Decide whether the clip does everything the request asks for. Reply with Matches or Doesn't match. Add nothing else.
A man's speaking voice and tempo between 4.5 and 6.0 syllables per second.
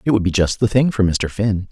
Matches